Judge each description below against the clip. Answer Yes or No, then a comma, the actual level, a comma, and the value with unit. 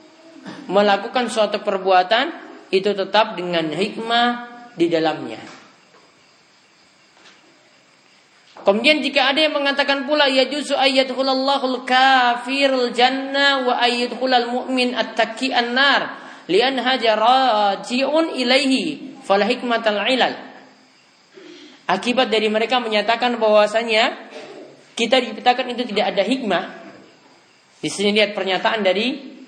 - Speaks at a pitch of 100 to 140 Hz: No, high, 245 Hz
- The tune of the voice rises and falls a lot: No, average, 3.7 semitones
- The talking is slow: Yes, slow, 75 wpm